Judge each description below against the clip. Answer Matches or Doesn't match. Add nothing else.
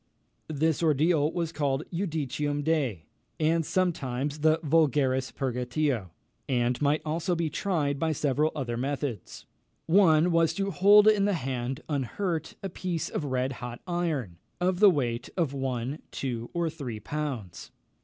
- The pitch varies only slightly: Doesn't match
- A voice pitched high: Doesn't match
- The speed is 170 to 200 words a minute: Doesn't match